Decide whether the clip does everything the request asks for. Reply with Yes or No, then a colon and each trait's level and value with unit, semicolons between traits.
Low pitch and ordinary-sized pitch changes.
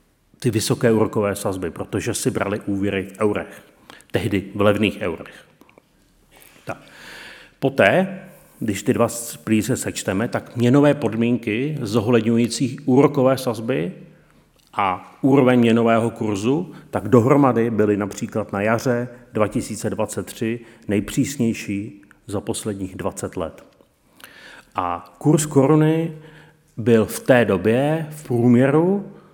Yes: low, 115 Hz; average, 4.2 semitones